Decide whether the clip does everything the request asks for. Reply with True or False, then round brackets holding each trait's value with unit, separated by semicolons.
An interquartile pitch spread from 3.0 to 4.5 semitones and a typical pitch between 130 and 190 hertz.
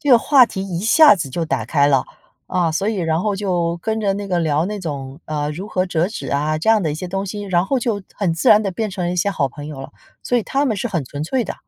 False (5.0 semitones; 185 Hz)